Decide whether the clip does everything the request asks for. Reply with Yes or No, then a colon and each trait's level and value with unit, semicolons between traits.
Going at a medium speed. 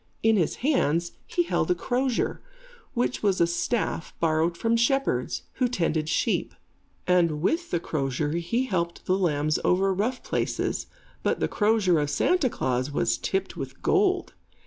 Yes: average, 155 wpm